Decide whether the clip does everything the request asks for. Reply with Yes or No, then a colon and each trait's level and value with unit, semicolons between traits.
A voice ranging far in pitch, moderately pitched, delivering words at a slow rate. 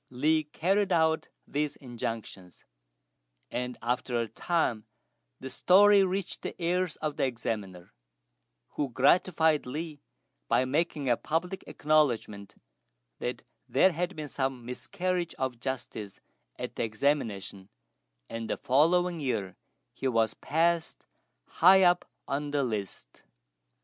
Yes: wide, 6.0 semitones; medium, 145 Hz; slow, 120 wpm